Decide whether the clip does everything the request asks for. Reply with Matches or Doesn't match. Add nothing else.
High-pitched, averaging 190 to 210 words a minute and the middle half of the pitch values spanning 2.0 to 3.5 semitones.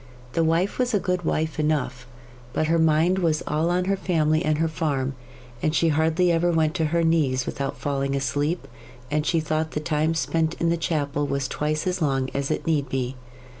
Doesn't match